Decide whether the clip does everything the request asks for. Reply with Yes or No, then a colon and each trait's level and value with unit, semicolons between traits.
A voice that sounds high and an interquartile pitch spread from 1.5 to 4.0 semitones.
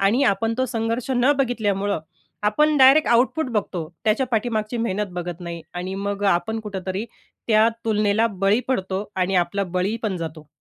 Yes: high, 210 Hz; average, 3.5 semitones